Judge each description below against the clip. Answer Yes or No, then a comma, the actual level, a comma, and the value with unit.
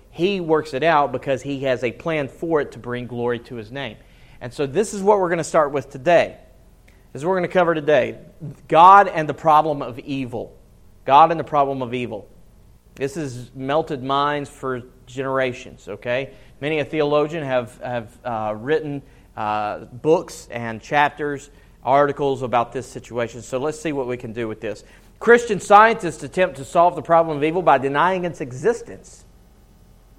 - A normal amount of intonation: Yes, average, 4.0 semitones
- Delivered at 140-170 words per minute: No, average, 185 wpm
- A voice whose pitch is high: No, medium, 140 Hz